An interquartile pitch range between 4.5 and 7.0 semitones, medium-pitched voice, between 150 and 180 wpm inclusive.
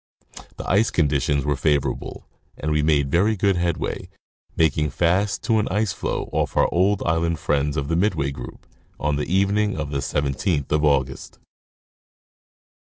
No: average, 4.8 semitones; very low, 80 Hz; average, 155 wpm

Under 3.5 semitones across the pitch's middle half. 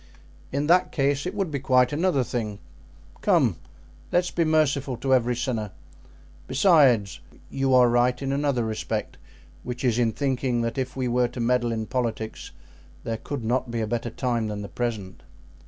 Yes: average, 2.9 semitones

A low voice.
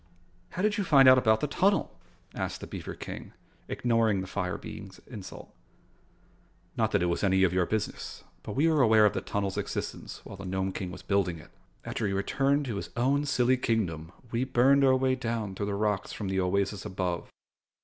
Yes: low, 105 Hz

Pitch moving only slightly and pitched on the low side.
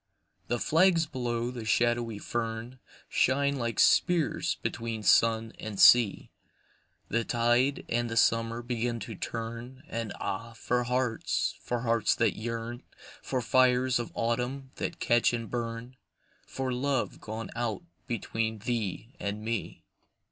Yes: narrow, 1.6 semitones; low, 120 Hz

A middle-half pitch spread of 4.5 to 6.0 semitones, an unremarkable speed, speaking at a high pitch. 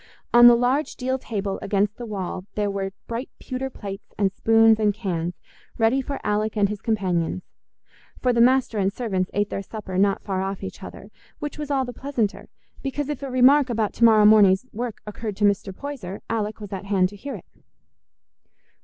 No: average, 3.9 semitones; average, 195 wpm; high, 215 Hz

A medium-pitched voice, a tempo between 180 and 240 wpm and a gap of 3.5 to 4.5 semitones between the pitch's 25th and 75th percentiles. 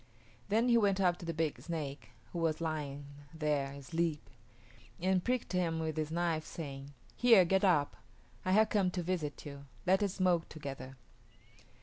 No: medium, 165 Hz; average, 165 wpm; average, 3.8 semitones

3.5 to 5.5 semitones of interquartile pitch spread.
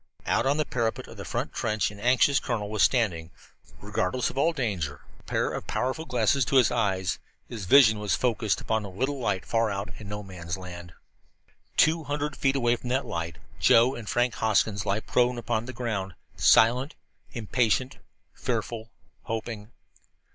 Yes: average, 3.9 semitones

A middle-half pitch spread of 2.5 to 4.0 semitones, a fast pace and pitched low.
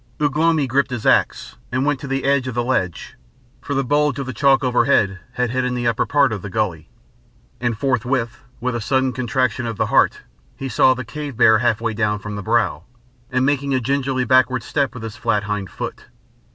Yes: average, 3.2 semitones; fast, 215 wpm; low, 125 Hz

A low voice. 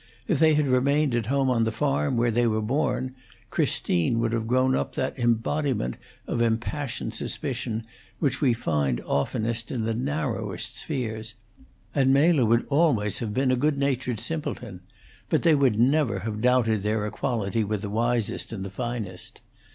Yes: low, 120 Hz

